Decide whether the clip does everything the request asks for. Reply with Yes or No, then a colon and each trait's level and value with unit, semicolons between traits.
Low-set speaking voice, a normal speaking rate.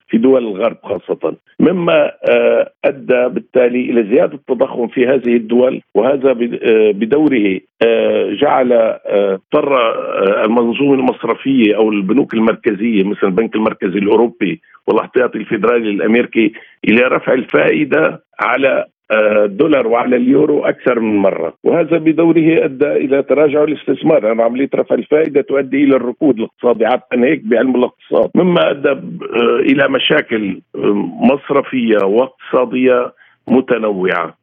Yes: low, 130 Hz; average, 110 wpm